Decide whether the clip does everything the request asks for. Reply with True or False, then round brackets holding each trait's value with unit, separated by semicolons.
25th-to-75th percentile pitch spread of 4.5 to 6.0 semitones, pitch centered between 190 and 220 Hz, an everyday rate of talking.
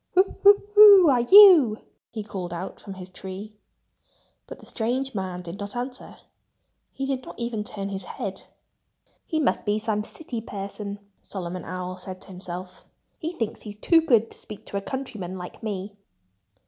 True (5.0 semitones; 210 Hz; 175 wpm)